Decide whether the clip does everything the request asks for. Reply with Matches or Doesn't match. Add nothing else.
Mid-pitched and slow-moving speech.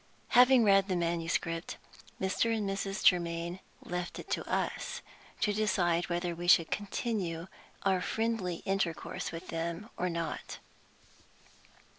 Matches